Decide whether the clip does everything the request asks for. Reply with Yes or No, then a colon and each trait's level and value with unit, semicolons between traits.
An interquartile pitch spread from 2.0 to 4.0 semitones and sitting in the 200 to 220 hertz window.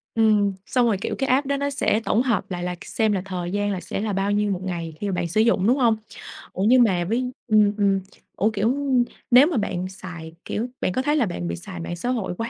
No: average, 4.4 semitones; high, 205 Hz